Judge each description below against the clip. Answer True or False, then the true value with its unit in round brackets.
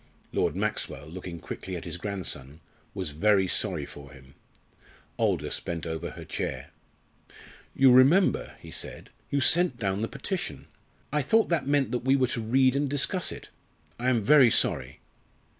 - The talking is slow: False (160 wpm)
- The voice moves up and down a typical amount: False (7.7 semitones)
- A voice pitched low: True (115 Hz)